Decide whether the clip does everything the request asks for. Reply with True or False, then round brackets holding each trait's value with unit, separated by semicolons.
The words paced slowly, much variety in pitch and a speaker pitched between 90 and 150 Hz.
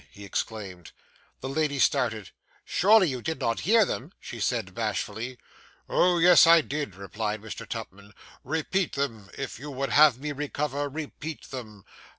False (155 wpm; 6.0 semitones; 140 Hz)